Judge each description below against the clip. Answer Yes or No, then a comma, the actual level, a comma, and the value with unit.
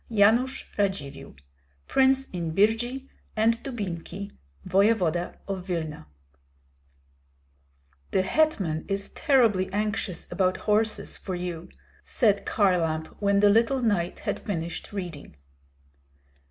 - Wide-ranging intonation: No, average, 4.1 semitones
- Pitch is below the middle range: No, high, 200 Hz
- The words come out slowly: Yes, slow, 100 wpm